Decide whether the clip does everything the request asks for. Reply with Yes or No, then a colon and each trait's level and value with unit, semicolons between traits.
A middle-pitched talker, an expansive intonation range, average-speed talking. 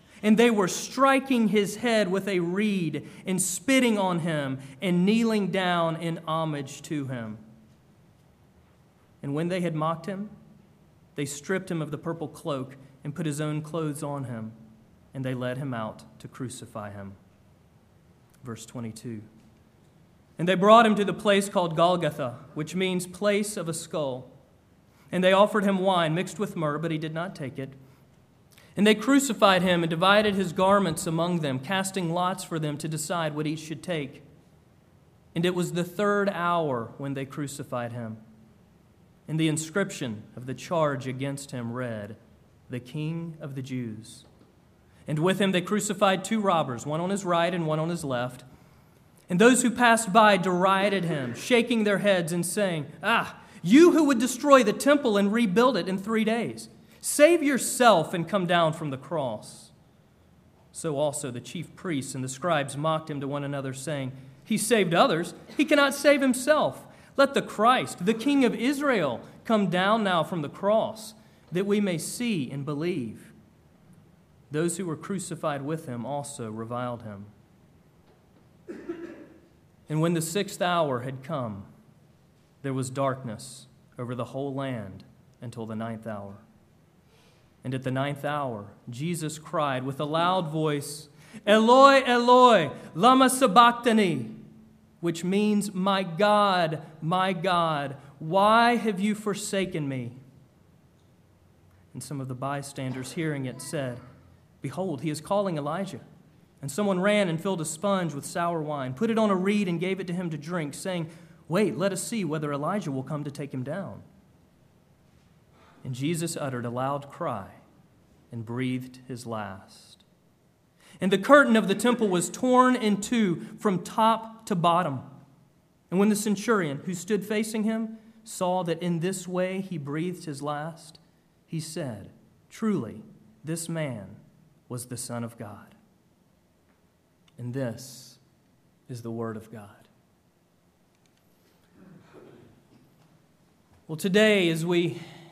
Yes: medium, 165 Hz; wide, 6.5 semitones; average, 155 wpm